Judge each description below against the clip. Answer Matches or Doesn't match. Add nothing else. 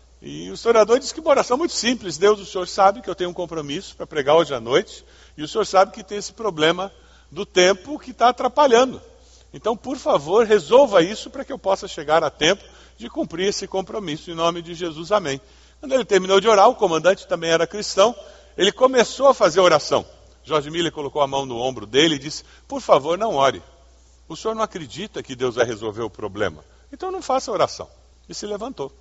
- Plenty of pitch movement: Matches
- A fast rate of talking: Matches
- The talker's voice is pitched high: Matches